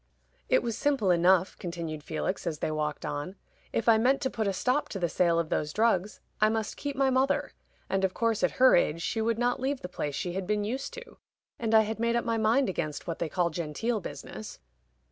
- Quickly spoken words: Yes, fast, 230 wpm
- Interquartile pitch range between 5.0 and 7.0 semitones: Yes, wide, 5.4 semitones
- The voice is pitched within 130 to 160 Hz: No, high, 210 Hz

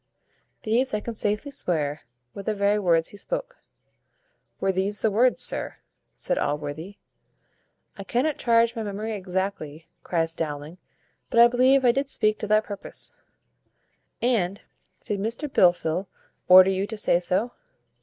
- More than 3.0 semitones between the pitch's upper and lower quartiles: Yes, average, 4.5 semitones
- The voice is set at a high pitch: Yes, high, 205 Hz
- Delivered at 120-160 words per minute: Yes, average, 145 wpm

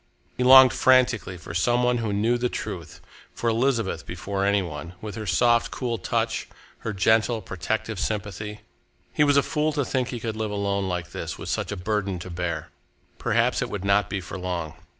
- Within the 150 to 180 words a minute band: No, average, 195 wpm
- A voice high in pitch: No, low, 105 Hz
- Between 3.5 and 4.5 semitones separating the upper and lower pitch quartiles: Yes, average, 4.2 semitones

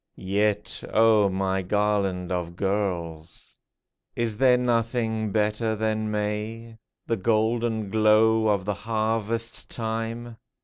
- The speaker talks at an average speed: No, slow, 105 wpm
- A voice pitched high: No, low, 110 Hz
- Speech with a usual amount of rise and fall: No, narrow, 2.0 semitones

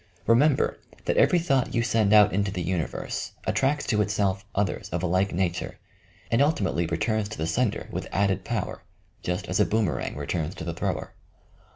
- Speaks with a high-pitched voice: No, low, 100 Hz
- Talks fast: No, average, 190 wpm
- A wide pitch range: No, average, 4.0 semitones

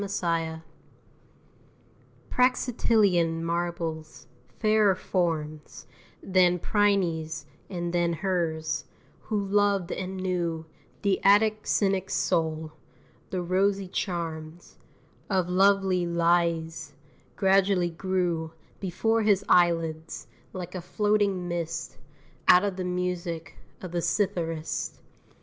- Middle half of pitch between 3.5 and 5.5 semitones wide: No, average, 2.8 semitones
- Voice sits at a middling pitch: Yes, medium, 180 Hz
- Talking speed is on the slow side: Yes, slow, 95 wpm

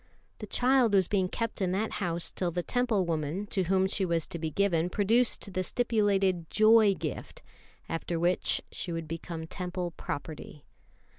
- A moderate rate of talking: Yes, average, 165 wpm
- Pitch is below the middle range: No, medium, 185 Hz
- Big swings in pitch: No, average, 3.5 semitones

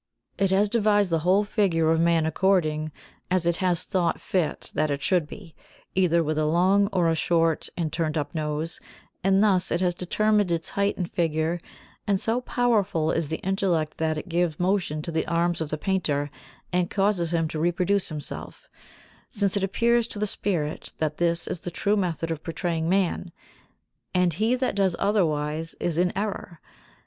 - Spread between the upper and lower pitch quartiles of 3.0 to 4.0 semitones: Yes, average, 3.3 semitones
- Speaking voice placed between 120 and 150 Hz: No, medium, 175 Hz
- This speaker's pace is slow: No, average, 180 wpm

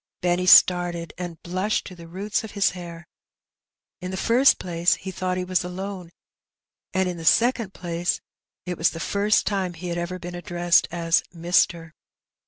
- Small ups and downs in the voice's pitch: Yes, narrow, 1.6 semitones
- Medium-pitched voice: Yes, medium, 180 Hz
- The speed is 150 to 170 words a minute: No, average, 185 wpm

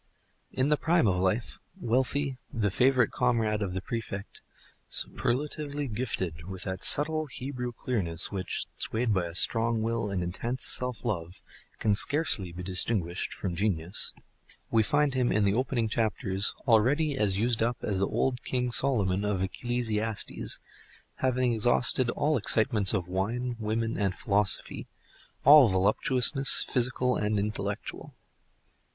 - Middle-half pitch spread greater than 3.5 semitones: Yes, average, 4.3 semitones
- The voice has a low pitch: Yes, low, 115 Hz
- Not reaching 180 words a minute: Yes, average, 140 wpm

